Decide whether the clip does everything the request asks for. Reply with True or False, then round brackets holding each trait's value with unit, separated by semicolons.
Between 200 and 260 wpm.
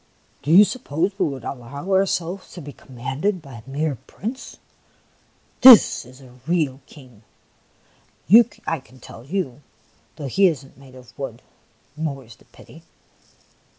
False (150 wpm)